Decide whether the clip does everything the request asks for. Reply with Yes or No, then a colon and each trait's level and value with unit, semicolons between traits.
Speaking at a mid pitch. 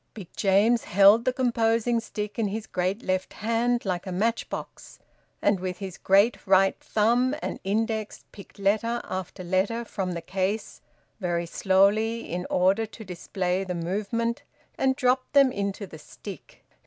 No: high, 205 Hz